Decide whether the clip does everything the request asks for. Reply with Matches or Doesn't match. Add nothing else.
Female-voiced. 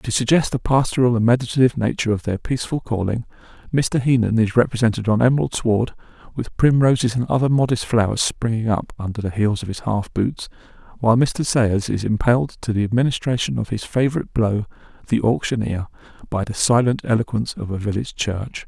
Doesn't match